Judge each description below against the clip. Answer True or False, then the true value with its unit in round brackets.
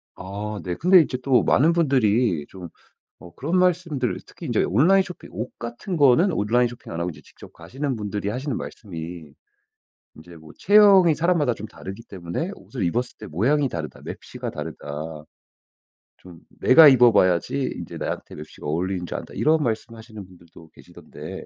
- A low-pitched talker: True (115 Hz)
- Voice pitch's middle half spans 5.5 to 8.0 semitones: False (8.5 semitones)